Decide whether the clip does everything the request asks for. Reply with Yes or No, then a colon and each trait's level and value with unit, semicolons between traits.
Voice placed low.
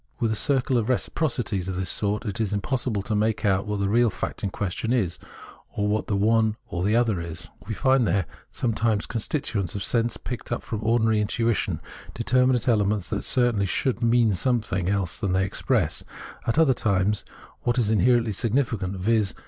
Yes: low, 110 Hz